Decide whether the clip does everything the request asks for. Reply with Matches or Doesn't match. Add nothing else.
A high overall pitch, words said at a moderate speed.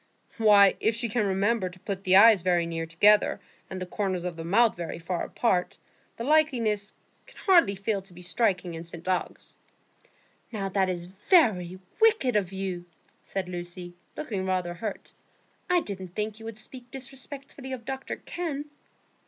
Matches